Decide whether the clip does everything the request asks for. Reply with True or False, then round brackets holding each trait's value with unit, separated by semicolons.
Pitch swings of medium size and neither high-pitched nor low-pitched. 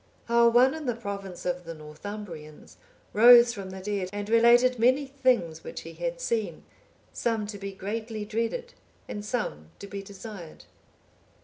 False (3.7 semitones; 210 Hz)